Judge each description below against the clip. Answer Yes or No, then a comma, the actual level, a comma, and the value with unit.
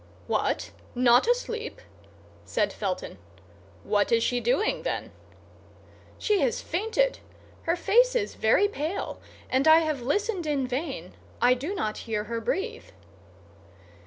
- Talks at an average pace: No, slow, 130 wpm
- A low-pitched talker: No, very high, 310 Hz